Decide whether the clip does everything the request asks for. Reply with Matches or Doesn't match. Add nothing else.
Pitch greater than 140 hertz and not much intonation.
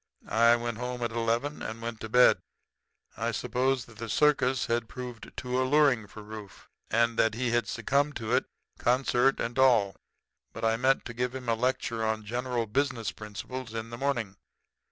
Doesn't match